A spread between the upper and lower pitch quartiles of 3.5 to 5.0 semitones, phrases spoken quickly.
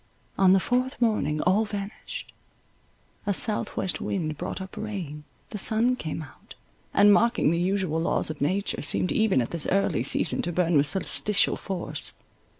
No: average, 4.4 semitones; average, 160 wpm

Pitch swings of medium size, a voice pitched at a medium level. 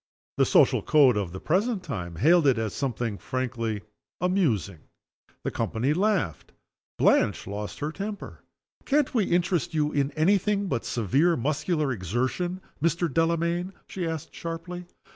No: wide, 7.3 semitones; medium, 155 Hz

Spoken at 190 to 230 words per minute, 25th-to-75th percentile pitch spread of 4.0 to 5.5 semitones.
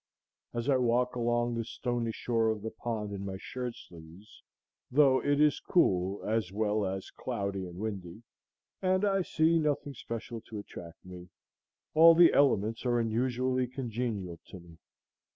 No: average, 155 wpm; average, 4.5 semitones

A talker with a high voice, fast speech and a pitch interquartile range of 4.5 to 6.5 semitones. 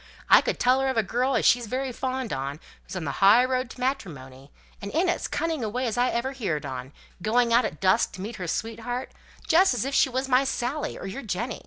Yes: high, 240 Hz; fast, 245 wpm; average, 5.2 semitones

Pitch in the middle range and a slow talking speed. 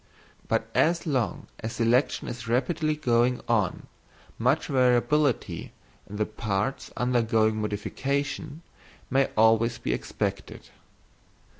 No: low, 120 Hz; slow, 105 wpm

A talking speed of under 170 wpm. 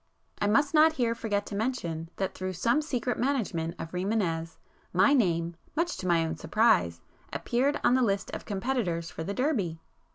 No: average, 175 wpm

